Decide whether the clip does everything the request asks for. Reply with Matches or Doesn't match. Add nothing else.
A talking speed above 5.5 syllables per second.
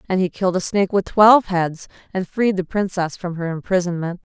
Matches